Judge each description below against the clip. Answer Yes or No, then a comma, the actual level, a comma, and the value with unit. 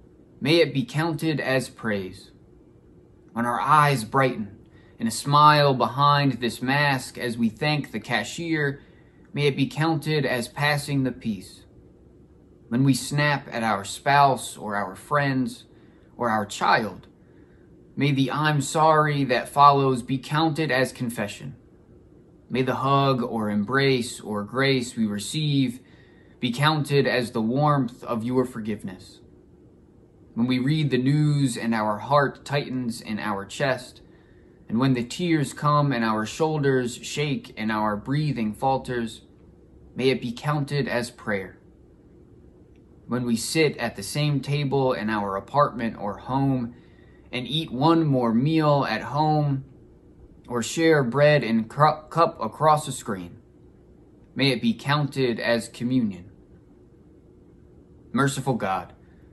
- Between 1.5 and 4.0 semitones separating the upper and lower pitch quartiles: No, average, 4.4 semitones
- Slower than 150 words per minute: Yes, slow, 135 wpm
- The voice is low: Yes, low, 130 Hz